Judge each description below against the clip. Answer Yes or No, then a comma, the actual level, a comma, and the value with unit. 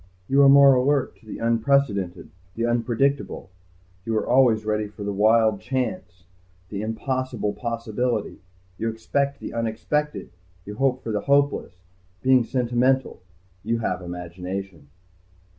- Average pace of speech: No, slow, 130 wpm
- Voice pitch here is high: No, low, 115 Hz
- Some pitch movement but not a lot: Yes, average, 4.0 semitones